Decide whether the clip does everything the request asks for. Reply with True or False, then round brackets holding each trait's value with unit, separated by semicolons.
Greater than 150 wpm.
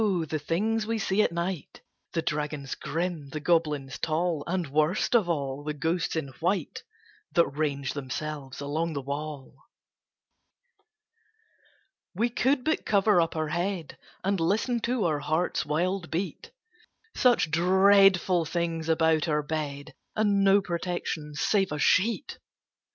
False (135 wpm)